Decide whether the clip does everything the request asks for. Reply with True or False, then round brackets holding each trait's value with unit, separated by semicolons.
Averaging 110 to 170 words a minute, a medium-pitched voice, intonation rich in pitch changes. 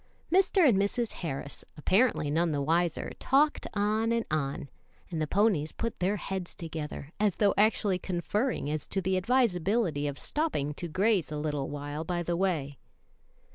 True (165 wpm; 180 Hz; 5.8 semitones)